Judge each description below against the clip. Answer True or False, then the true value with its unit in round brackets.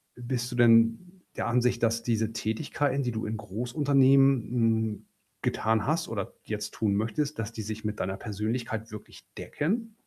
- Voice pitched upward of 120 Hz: False (115 Hz)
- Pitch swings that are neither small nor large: True (3.1 semitones)